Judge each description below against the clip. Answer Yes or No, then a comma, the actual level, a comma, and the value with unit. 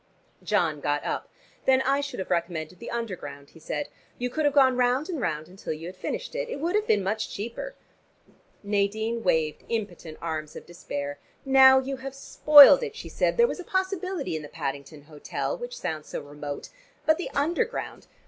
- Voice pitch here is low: No, high, 230 Hz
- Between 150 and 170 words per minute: No, average, 185 wpm